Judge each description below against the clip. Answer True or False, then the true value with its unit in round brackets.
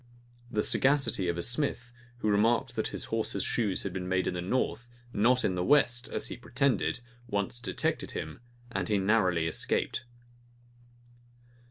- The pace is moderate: True (160 wpm)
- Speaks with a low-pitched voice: True (105 Hz)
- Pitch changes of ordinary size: True (4.8 semitones)